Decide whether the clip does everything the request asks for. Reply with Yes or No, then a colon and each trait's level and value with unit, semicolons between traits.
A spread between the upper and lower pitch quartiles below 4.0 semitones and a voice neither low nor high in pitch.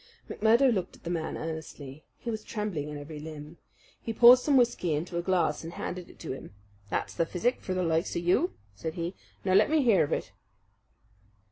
No: average, 5.2 semitones; medium, 175 Hz